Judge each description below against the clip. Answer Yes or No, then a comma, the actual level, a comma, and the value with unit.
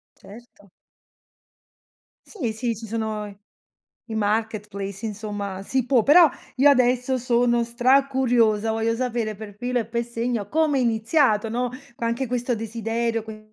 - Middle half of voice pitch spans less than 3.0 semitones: Yes, narrow, 2.4 semitones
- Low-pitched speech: No, high, 230 Hz